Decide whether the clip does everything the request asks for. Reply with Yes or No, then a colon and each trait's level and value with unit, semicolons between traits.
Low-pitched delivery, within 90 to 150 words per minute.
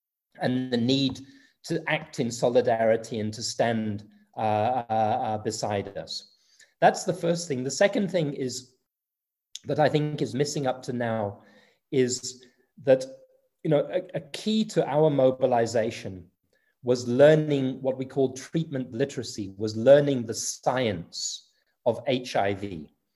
Yes: low, 130 Hz; slow, 135 wpm